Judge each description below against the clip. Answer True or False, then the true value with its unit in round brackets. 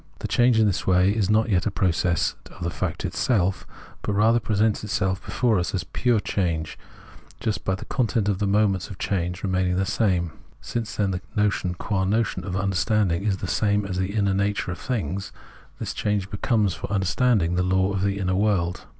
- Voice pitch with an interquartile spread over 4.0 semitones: False (2.4 semitones)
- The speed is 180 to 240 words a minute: True (200 wpm)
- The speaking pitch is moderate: False (100 Hz)